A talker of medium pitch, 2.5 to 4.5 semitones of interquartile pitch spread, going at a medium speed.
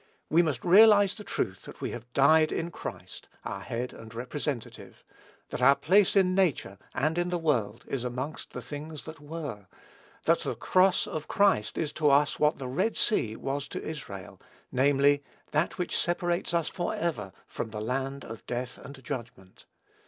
No: medium, 145 Hz; average, 5.3 semitones; average, 175 wpm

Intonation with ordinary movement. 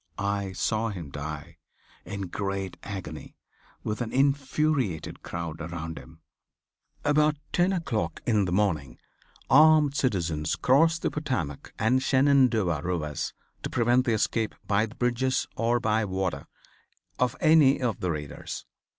No: wide, 7.3 semitones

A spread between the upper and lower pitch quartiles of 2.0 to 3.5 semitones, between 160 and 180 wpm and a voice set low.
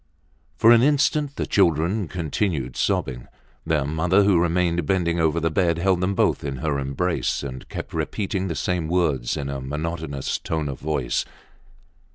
No: average, 4.1 semitones; average, 165 wpm; very low, 85 Hz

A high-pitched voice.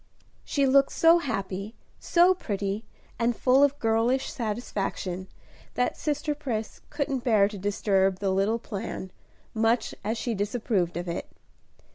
Yes: high, 225 Hz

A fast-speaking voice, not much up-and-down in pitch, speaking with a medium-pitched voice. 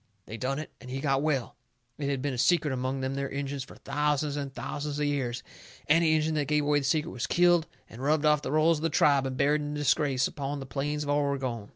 Yes: fast, 245 wpm; narrow, 1.9 semitones; medium, 145 Hz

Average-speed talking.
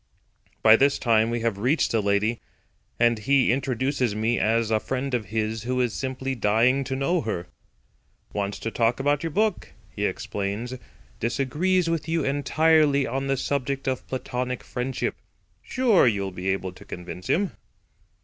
Yes: average, 160 wpm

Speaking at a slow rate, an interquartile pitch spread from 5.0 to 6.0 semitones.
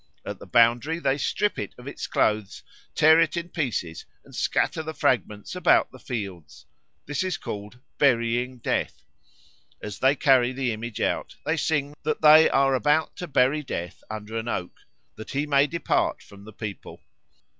No: average, 170 wpm; wide, 5.5 semitones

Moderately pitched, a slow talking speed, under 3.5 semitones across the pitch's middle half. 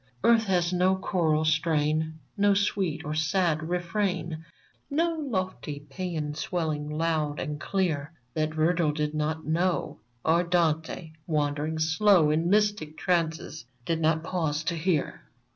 Yes: medium, 160 Hz; slow, 130 wpm; average, 2.9 semitones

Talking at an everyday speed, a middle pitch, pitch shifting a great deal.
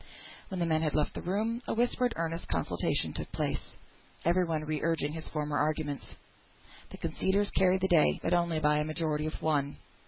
No: average, 190 wpm; medium, 160 Hz; average, 3.1 semitones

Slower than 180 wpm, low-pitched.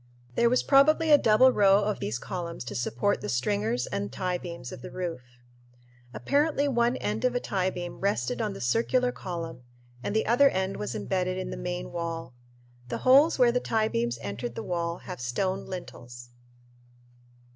No: average, 170 wpm; medium, 185 Hz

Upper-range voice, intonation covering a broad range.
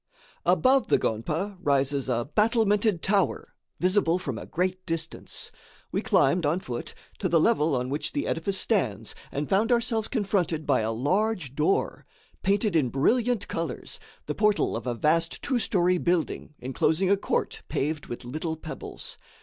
No: medium, 170 Hz; wide, 6.1 semitones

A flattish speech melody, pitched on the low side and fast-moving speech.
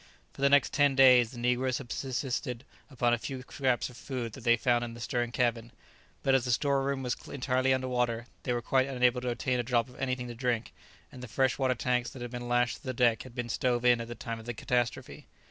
Yes: narrow, 1.5 semitones; low, 125 Hz; fast, 250 wpm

